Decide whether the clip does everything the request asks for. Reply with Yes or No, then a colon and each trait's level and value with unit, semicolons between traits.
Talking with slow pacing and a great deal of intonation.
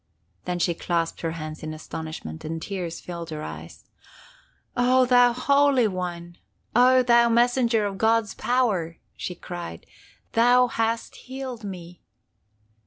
Yes: slow, 130 wpm; wide, 6.5 semitones